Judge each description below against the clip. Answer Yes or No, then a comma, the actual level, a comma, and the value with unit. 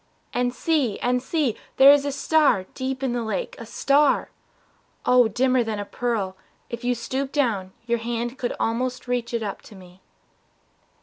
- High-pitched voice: Yes, high, 245 Hz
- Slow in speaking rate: No, average, 175 wpm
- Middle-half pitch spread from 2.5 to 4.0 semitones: Yes, average, 2.8 semitones